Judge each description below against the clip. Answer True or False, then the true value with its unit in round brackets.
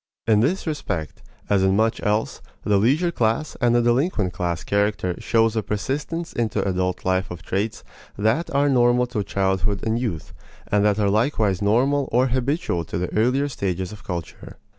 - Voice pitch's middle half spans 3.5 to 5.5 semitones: True (4.4 semitones)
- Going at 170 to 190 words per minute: True (175 wpm)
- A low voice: True (110 Hz)